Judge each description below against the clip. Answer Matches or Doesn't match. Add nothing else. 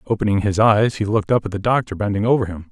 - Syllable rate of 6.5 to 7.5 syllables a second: Matches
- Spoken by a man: Matches